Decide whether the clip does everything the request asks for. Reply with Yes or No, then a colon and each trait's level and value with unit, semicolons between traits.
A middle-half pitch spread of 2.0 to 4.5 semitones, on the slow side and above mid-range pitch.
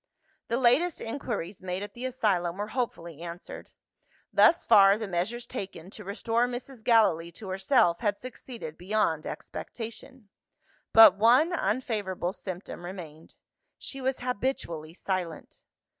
No: wide, 5.4 semitones; slow, 130 wpm; high, 205 Hz